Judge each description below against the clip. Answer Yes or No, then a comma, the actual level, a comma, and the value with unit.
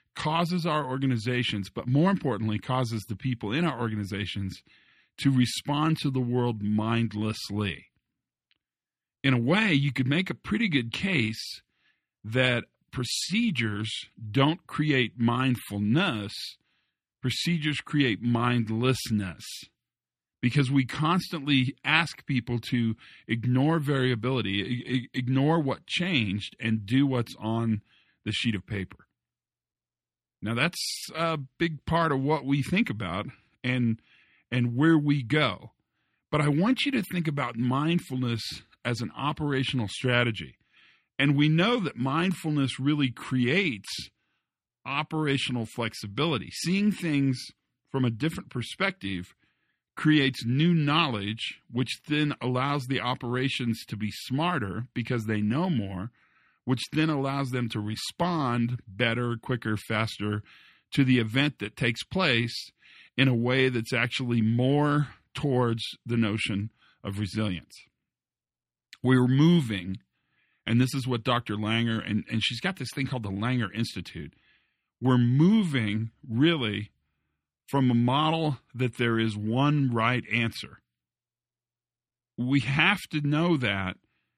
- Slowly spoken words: Yes, slow, 125 wpm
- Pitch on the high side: No, low, 125 Hz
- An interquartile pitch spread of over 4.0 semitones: Yes, average, 4.5 semitones